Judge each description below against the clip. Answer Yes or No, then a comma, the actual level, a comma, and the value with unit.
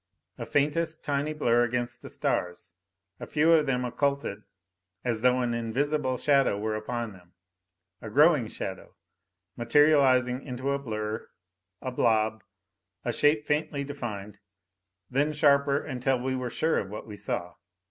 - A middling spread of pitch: Yes, average, 4.4 semitones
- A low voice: Yes, low, 125 Hz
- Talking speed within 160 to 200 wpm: No, average, 145 wpm